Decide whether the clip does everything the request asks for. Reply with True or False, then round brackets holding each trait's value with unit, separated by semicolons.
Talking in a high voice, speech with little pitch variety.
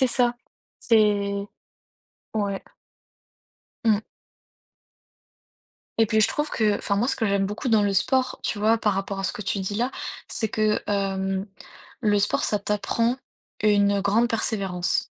True (210 Hz; 1.9 semitones)